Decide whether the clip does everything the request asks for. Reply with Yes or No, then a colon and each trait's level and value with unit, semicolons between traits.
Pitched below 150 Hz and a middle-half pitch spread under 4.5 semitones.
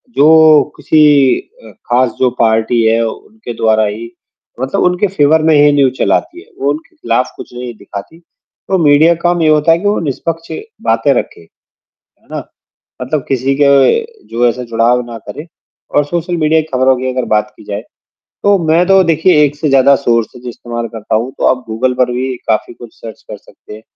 No: low, 135 Hz; average, 5.1 semitones